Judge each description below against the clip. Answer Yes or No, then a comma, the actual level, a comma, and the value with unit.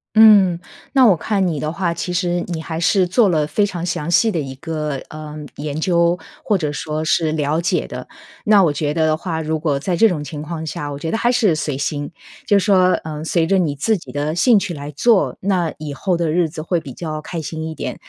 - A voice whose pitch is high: No, medium, 165 Hz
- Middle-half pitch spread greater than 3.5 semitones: No, average, 3.2 semitones